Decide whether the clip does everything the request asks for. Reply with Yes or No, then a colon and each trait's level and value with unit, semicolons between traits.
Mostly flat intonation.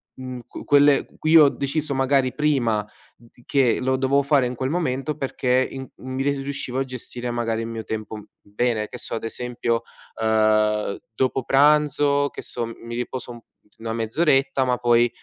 No: average, 3.1 semitones